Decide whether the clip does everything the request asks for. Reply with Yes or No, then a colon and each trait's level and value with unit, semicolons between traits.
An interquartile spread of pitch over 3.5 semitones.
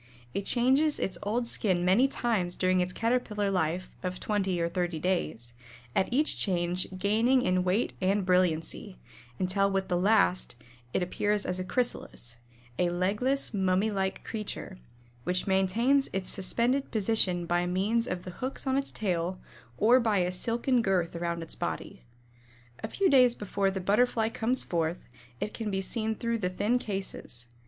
Yes: average, 4.1 semitones